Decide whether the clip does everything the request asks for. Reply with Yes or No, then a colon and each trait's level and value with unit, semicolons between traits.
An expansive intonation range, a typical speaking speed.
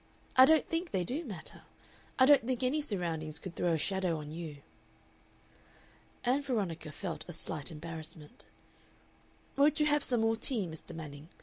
Yes: wide, 8.3 semitones; average, 165 wpm